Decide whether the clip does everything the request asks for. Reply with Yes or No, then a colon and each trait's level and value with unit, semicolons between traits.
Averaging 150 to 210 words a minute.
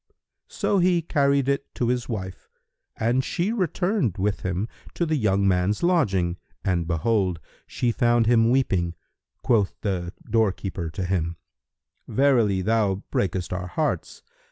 No: slow, 135 wpm